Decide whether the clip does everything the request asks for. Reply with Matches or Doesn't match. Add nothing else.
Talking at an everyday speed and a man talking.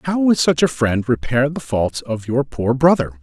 Doesn't match